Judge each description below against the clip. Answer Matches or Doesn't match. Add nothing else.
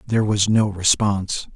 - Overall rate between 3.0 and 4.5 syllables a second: Doesn't match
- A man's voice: Matches